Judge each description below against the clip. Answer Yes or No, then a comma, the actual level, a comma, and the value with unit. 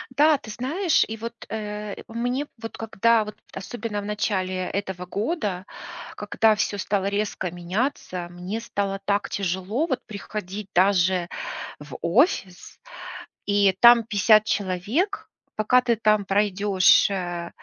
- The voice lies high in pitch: Yes, high, 205 Hz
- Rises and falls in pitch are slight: No, average, 3.1 semitones